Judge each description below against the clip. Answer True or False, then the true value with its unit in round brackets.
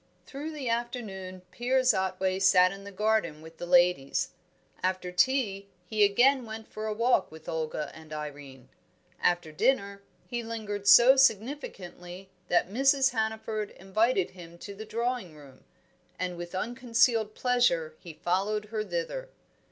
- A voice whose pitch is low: False (200 Hz)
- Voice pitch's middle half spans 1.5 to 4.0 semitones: False (5.0 semitones)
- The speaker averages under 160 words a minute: True (145 wpm)